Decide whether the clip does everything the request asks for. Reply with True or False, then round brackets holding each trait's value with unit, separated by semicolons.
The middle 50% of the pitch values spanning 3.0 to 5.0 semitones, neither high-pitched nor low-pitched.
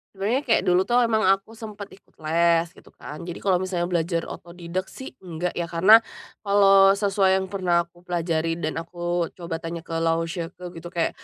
False (2.6 semitones; 175 Hz)